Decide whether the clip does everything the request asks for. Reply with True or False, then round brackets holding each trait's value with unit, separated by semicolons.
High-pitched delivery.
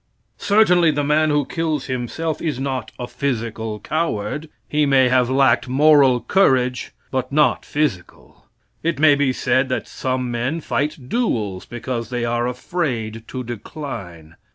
False (130 Hz)